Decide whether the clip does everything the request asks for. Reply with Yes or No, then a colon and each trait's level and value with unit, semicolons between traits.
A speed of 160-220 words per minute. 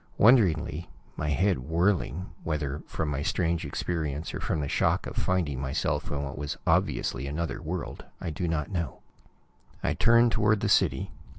Yes: average, 165 wpm